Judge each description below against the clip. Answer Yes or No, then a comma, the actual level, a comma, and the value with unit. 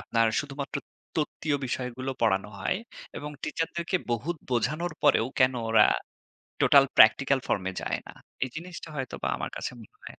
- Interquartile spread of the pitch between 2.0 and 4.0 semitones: No, average, 4.9 semitones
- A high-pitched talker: No, low, 135 Hz